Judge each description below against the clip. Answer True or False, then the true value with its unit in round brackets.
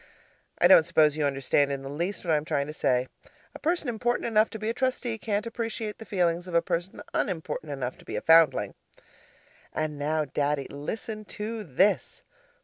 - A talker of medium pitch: True (170 Hz)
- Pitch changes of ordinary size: False (6.8 semitones)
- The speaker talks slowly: False (195 wpm)